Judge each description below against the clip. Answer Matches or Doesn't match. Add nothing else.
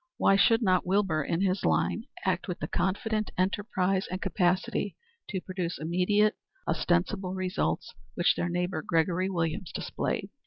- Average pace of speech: Matches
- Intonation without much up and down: Matches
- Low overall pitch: Doesn't match